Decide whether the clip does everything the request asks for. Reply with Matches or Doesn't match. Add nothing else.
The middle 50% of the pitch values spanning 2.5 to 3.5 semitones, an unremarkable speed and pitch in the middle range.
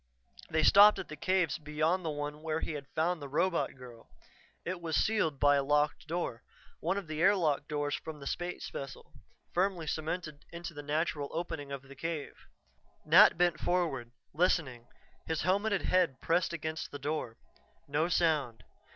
Matches